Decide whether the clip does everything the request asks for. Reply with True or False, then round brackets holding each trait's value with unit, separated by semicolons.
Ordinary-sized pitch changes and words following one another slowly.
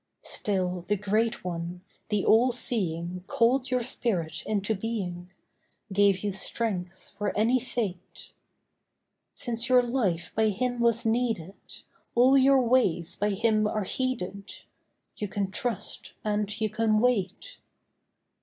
True (3.9 semitones; 125 wpm)